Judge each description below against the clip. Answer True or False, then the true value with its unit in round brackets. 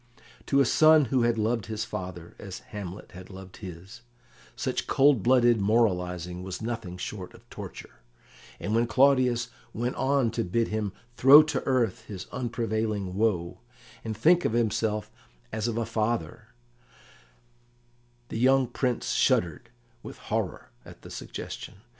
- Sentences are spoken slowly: False (145 wpm)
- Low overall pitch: True (110 Hz)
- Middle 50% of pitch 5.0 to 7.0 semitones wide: False (4.0 semitones)